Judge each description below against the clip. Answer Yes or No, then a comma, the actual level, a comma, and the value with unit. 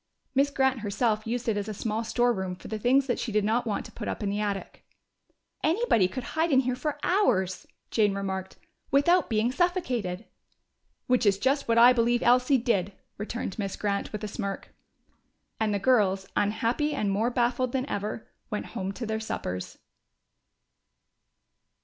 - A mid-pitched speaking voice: No, high, 225 Hz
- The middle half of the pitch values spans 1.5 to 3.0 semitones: No, average, 3.9 semitones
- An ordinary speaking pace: Yes, average, 170 wpm